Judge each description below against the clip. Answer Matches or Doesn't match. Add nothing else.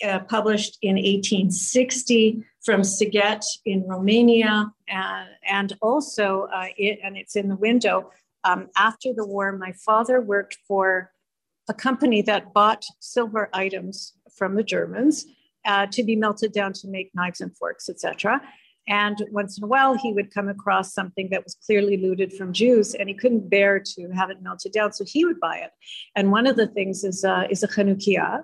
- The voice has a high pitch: Matches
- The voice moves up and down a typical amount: Doesn't match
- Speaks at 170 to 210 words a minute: Matches